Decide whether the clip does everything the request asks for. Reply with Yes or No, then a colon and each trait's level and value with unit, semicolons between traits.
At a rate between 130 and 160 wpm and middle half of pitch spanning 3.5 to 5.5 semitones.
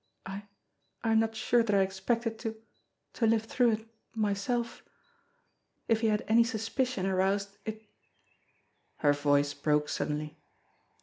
No: average, 150 wpm; average, 3.0 semitones